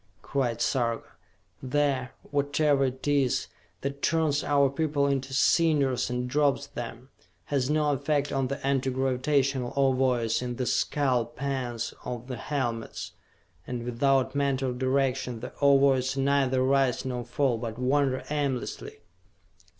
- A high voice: No, low, 135 Hz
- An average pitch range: No, narrow, 2.1 semitones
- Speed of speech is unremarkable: No, slow, 130 wpm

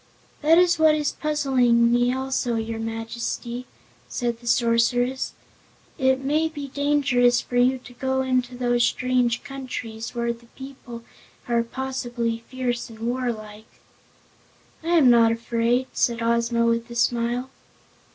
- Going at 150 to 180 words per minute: No, slow, 135 wpm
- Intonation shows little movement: Yes, narrow, 2.1 semitones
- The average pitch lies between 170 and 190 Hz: No, high, 245 Hz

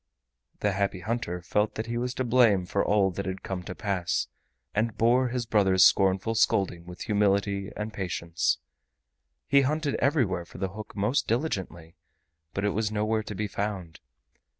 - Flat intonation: No, average, 3.3 semitones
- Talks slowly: No, average, 170 wpm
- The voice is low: Yes, low, 105 Hz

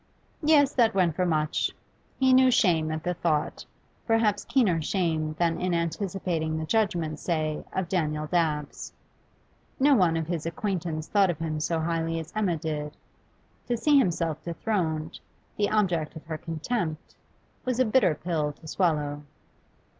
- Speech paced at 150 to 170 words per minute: Yes, average, 155 wpm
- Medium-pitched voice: Yes, medium, 170 Hz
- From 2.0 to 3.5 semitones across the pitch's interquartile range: No, average, 4.2 semitones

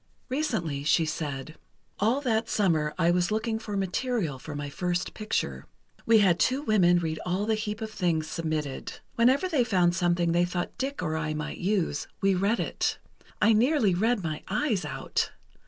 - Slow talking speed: No, average, 175 wpm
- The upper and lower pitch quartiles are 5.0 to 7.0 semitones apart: Yes, wide, 5.4 semitones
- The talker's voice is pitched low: No, medium, 185 Hz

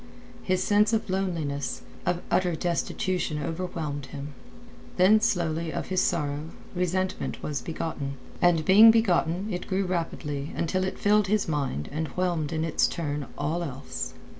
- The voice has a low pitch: No, medium, 170 Hz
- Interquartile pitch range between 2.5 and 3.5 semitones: No, average, 4.0 semitones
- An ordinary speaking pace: Yes, average, 145 wpm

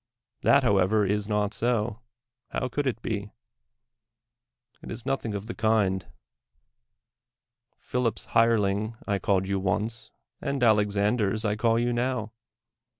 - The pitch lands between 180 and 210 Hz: No, low, 110 Hz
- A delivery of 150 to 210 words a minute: No, average, 140 wpm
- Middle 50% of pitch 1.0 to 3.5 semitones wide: Yes, average, 2.7 semitones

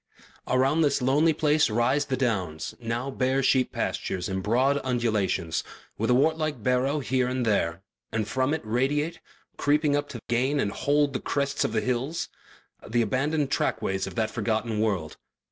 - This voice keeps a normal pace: Yes, average, 170 wpm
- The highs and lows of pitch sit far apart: No, average, 4.3 semitones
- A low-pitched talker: Yes, low, 130 Hz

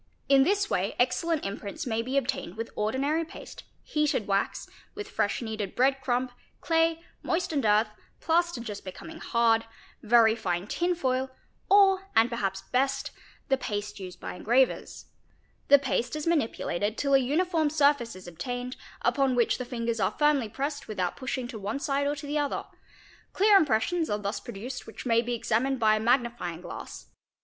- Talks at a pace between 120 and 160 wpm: No, average, 175 wpm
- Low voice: No, very high, 250 Hz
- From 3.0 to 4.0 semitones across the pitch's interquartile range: No, average, 4.9 semitones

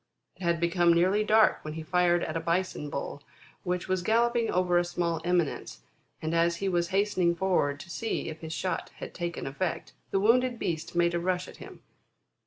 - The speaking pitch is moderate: Yes, medium, 175 Hz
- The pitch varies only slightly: Yes, narrow, 1.9 semitones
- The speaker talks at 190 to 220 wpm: Yes, average, 195 wpm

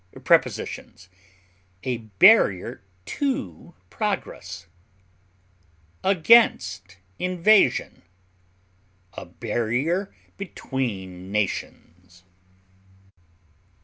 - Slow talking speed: Yes, slow, 50 wpm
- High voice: No, low, 115 Hz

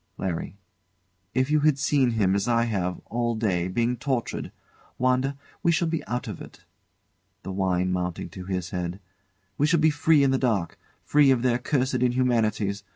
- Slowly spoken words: No, average, 175 wpm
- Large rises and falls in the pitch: Yes, wide, 5.9 semitones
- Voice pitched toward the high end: No, low, 120 Hz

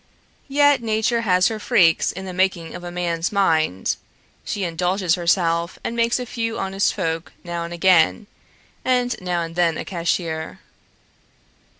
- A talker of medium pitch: Yes, medium, 180 Hz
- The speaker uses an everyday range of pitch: Yes, average, 4.1 semitones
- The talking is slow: No, average, 155 wpm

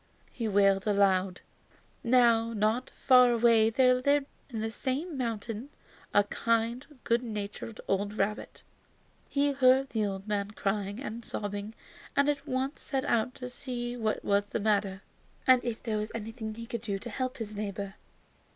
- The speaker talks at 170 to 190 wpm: No, average, 160 wpm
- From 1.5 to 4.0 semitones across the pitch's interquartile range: Yes, average, 3.6 semitones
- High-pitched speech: Yes, high, 225 Hz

